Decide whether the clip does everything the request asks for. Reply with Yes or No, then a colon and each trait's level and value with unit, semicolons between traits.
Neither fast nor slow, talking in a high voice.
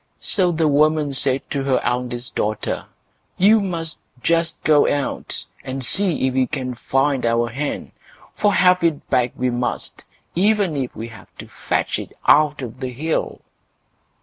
No: average, 160 wpm; medium, 140 Hz